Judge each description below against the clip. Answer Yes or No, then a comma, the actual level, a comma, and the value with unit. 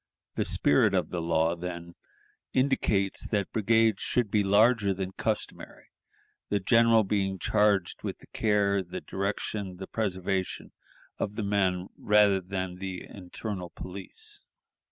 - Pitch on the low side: Yes, low, 100 Hz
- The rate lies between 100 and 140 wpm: Yes, slow, 135 wpm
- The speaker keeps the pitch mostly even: Yes, narrow, 2.3 semitones